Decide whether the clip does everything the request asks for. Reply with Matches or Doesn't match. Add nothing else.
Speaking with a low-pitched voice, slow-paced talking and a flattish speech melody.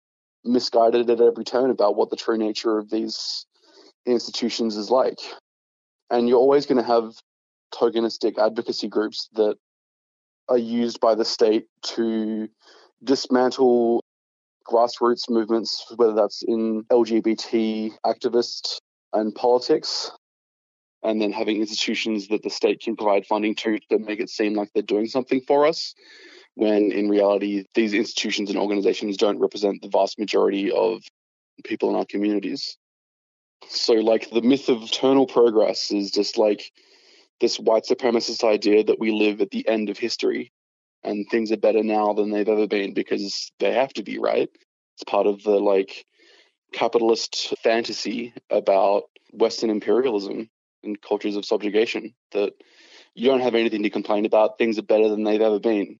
Doesn't match